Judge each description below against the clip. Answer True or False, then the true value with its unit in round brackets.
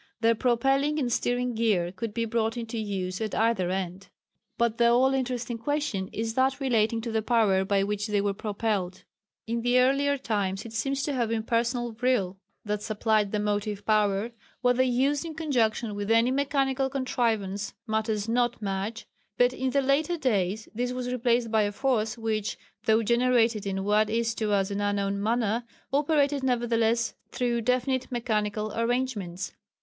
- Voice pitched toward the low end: False (230 Hz)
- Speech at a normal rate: True (170 wpm)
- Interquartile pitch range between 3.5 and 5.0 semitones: False (3.1 semitones)